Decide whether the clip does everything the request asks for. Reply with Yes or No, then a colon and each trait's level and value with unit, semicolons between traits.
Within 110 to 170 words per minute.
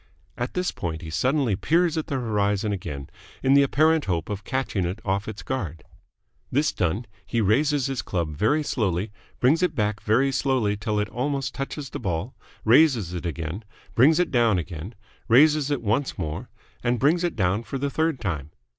No: average, 185 wpm